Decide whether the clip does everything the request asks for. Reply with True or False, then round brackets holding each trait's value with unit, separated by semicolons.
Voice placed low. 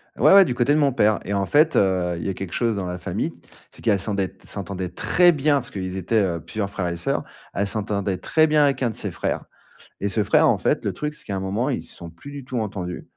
True (100 Hz)